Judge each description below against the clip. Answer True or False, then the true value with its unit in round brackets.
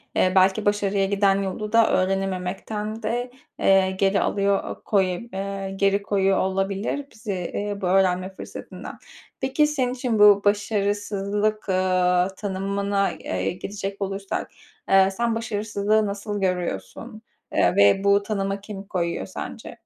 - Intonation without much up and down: True (1.5 semitones)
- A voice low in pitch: False (200 Hz)